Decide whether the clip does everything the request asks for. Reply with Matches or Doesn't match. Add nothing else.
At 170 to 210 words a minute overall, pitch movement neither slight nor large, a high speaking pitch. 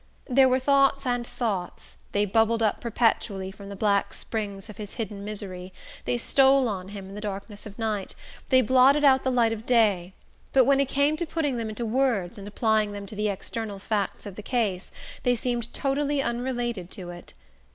Matches